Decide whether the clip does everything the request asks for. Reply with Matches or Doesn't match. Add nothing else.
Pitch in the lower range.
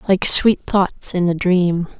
Doesn't match